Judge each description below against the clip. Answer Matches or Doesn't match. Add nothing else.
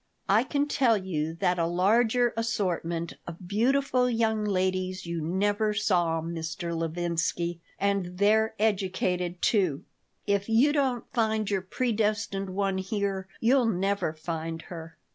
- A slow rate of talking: Matches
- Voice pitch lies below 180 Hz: Doesn't match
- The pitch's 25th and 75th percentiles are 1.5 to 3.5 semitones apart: Doesn't match